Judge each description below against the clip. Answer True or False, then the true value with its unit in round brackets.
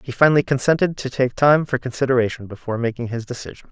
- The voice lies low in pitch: True (130 Hz)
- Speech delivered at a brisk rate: False (195 wpm)